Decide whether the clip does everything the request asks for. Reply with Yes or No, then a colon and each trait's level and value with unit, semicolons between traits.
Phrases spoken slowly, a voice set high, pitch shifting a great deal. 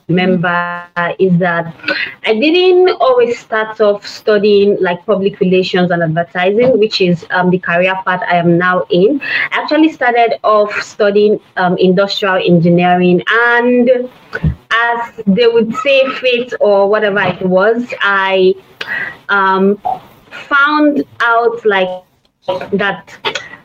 No: slow, 125 wpm; high, 200 Hz; average, 4.3 semitones